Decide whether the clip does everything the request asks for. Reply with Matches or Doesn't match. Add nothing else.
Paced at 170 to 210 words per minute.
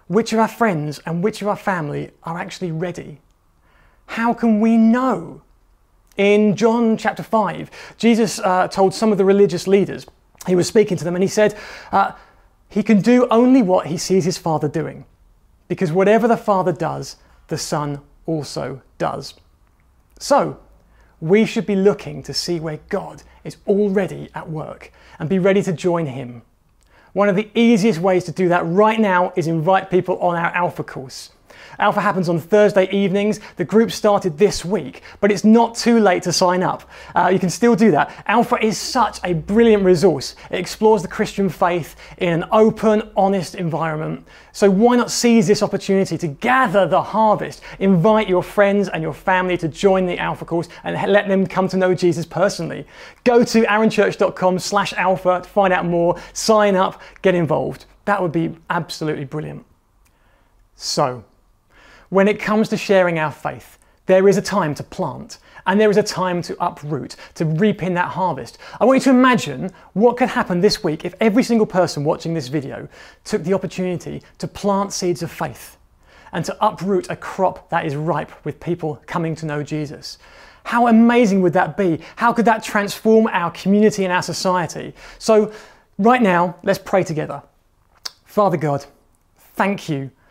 Matches